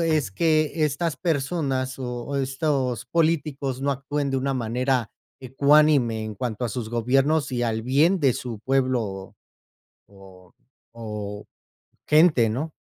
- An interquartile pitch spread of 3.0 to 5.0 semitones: Yes, average, 4.0 semitones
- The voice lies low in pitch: Yes, low, 130 Hz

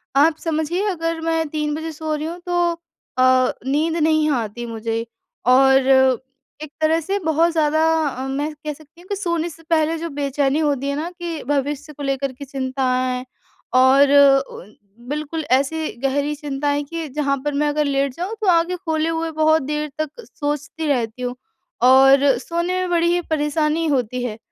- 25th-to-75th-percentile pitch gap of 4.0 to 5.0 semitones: No, average, 3.0 semitones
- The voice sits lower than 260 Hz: No, very high, 300 Hz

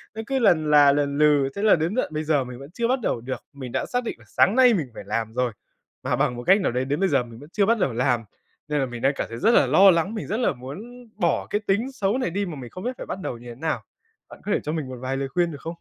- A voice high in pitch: No, medium, 155 Hz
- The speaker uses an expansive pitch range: Yes, wide, 7.6 semitones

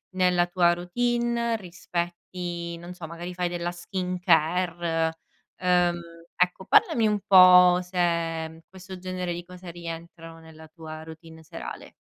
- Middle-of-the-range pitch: Yes, medium, 175 Hz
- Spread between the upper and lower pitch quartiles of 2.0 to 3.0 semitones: No, narrow, 1.5 semitones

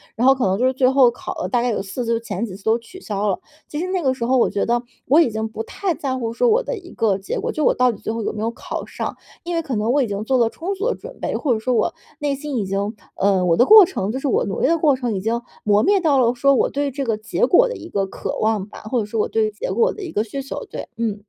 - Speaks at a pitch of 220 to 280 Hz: Yes, high, 240 Hz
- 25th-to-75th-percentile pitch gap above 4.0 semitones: Yes, average, 4.9 semitones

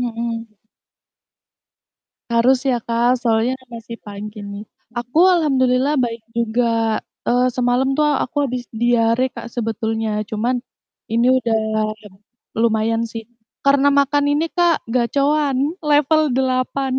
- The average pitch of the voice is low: No, high, 245 Hz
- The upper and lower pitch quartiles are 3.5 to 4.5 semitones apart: No, average, 2.9 semitones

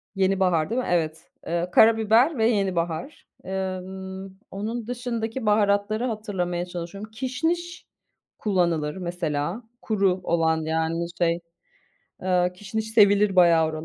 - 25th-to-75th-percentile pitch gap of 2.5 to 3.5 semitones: No, average, 4.2 semitones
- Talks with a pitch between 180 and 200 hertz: Yes, high, 190 Hz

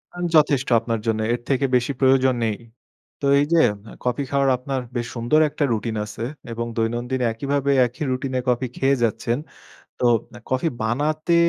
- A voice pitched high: No, low, 130 Hz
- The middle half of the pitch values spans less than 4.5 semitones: Yes, average, 2.9 semitones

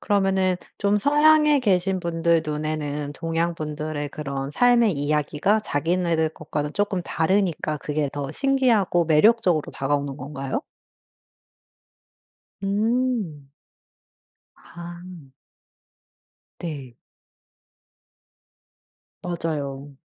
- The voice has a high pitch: No, medium, 165 Hz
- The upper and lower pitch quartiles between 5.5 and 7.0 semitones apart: No, average, 5.1 semitones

